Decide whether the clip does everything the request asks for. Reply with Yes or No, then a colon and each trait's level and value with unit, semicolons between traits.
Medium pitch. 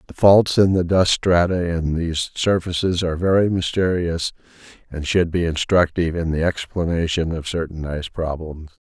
No: very low, 85 Hz